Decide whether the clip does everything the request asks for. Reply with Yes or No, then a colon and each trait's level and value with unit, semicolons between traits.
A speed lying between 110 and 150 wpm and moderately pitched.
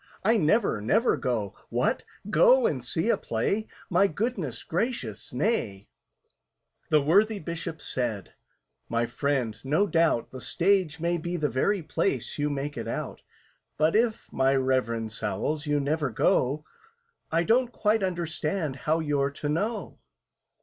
Yes: average, 140 wpm; medium, 155 Hz